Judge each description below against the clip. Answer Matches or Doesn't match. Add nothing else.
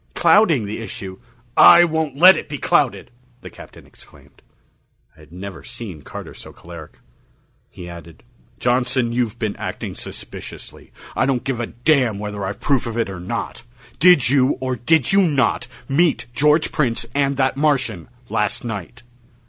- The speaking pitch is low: Matches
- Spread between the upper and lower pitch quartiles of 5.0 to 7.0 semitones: Matches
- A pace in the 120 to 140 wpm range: Doesn't match